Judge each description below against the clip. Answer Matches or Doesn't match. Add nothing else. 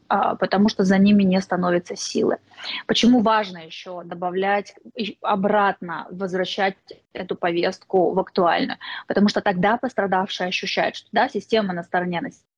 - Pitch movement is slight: Matches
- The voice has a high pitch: Matches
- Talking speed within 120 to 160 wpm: Matches